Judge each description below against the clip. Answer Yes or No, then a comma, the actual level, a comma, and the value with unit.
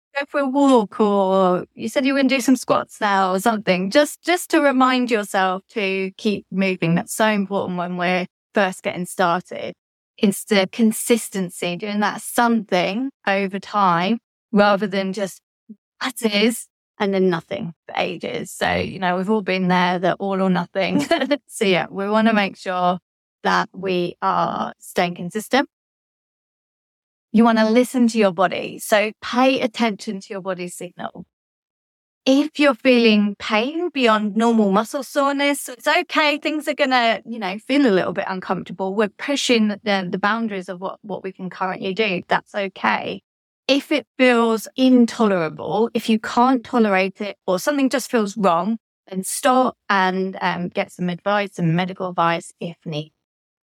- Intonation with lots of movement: No, average, 4.3 semitones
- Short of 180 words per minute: Yes, average, 165 wpm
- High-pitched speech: Yes, high, 205 Hz